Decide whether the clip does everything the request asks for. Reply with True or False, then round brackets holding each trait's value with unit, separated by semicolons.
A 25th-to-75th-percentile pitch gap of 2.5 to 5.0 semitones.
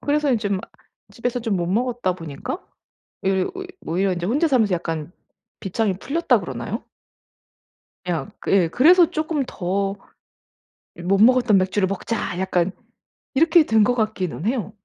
False (5.5 semitones)